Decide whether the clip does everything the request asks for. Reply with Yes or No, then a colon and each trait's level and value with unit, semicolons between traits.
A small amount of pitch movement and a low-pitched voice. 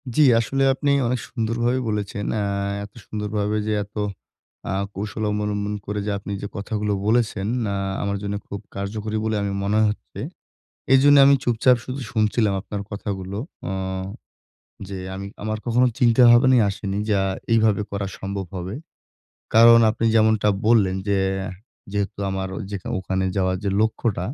Yes: narrow, 2.3 semitones; low, 105 Hz